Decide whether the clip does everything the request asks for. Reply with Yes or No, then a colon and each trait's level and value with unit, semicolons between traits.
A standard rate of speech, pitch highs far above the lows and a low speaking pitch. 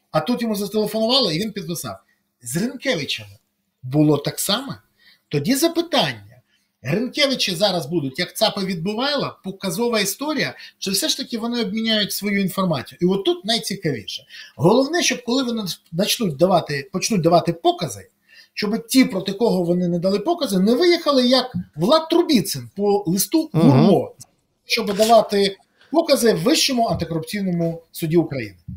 No: average, 140 wpm; wide, 5.8 semitones; high, 205 Hz